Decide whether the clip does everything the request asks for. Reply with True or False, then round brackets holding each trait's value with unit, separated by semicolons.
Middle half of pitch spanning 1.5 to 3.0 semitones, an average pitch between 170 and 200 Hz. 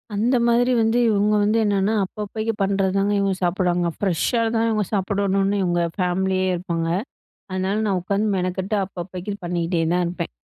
True (2.5 semitones; 195 Hz)